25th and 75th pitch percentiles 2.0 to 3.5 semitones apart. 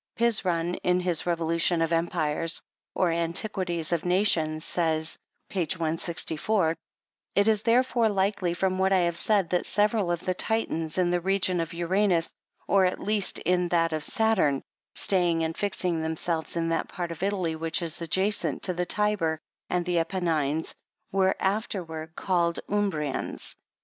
Yes: average, 2.7 semitones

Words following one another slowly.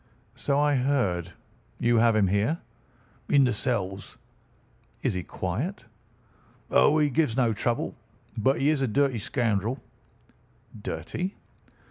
Yes: slow, 125 wpm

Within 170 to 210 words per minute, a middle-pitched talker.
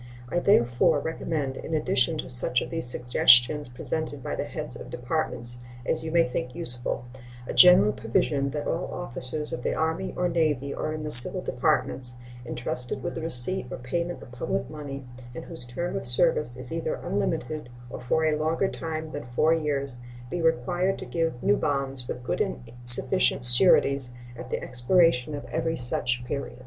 Yes: average, 180 wpm; medium, 145 Hz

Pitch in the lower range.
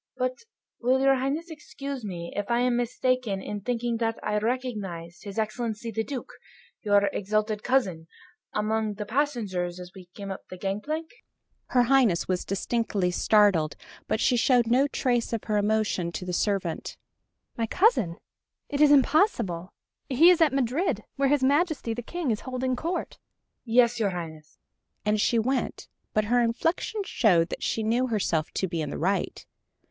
No: high, 225 Hz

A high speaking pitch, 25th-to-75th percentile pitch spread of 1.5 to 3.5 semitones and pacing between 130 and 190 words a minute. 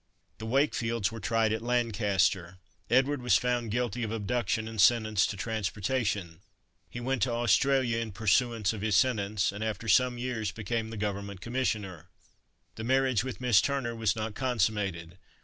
No: low, 110 Hz; average, 3.1 semitones; average, 160 wpm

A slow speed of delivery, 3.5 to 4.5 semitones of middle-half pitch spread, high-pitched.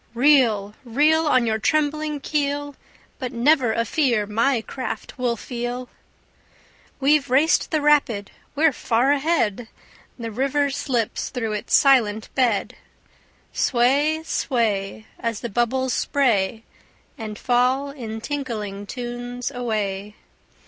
Yes: slow, 115 wpm; average, 4.1 semitones; high, 245 Hz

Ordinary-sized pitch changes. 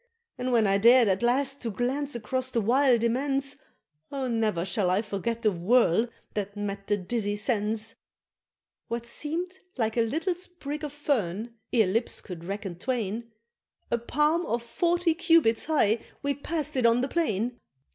Yes: average, 4.9 semitones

